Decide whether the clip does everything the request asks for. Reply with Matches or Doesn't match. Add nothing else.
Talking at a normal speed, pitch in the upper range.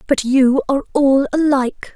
Matches